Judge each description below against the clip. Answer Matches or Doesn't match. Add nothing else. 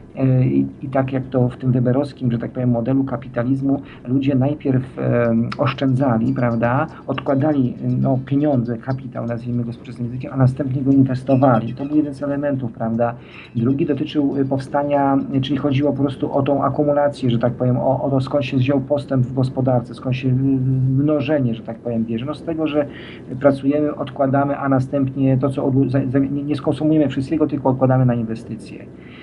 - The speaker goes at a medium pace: Doesn't match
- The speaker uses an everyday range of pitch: Doesn't match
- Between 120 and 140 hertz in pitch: Matches